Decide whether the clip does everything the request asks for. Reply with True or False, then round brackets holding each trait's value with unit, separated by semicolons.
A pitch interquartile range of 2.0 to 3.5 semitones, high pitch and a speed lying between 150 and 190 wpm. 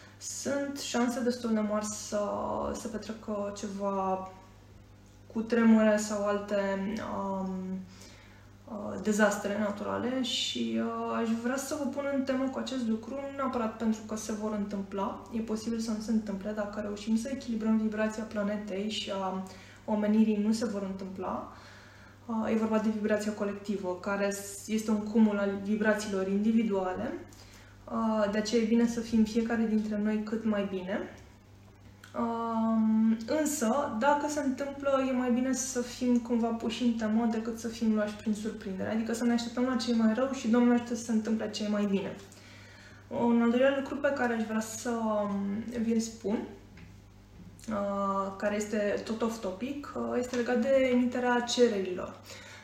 True (3.0 semitones; 215 Hz; 160 wpm)